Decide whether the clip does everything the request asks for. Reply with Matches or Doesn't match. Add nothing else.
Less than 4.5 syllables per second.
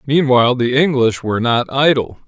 Doesn't match